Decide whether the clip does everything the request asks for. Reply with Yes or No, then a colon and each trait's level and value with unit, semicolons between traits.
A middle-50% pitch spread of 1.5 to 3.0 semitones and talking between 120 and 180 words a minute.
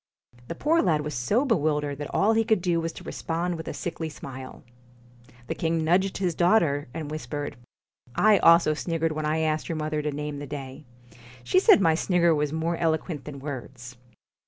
No: average, 2.7 semitones; average, 195 wpm